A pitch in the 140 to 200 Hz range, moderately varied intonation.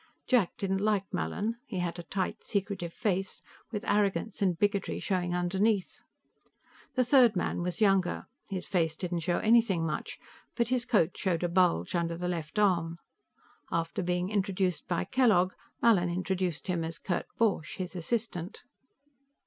Yes: medium, 185 Hz; average, 3.1 semitones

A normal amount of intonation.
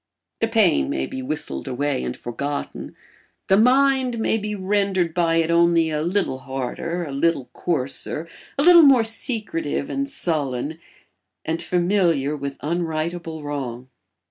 No: wide, 6.2 semitones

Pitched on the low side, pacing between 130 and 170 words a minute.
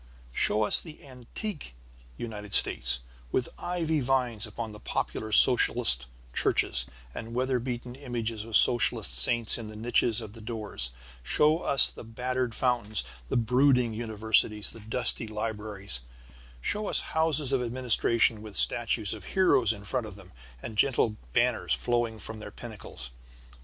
Yes: low, 115 Hz; average, 145 wpm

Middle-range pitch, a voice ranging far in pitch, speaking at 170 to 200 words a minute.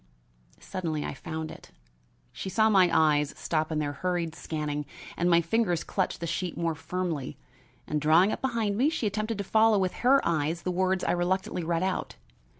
No: medium, 175 Hz; average, 3.5 semitones; average, 185 wpm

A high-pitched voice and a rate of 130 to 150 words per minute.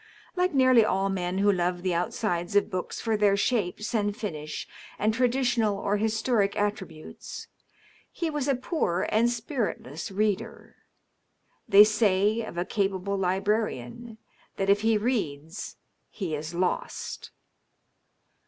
Yes: high, 205 Hz; slow, 135 wpm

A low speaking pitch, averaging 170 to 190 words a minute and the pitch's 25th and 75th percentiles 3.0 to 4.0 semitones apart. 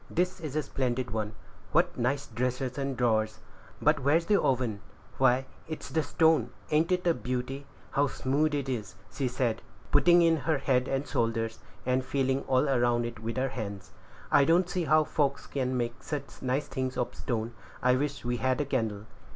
Yes: low, 130 Hz; average, 185 wpm; average, 3.3 semitones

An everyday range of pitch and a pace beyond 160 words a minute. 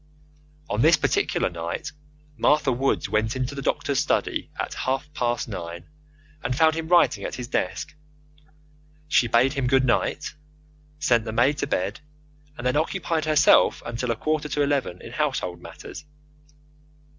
No: average, 4.7 semitones; average, 155 wpm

